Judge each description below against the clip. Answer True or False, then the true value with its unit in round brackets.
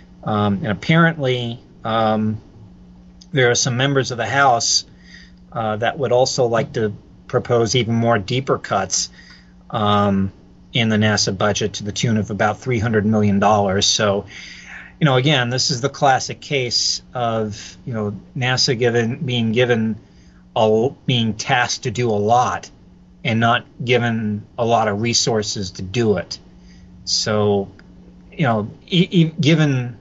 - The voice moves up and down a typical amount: True (3.8 semitones)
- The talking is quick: False (150 wpm)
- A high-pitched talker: False (110 Hz)